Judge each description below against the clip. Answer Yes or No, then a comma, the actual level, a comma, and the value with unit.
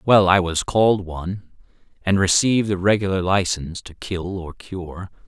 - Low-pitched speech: Yes, very low, 95 Hz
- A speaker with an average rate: Yes, average, 160 wpm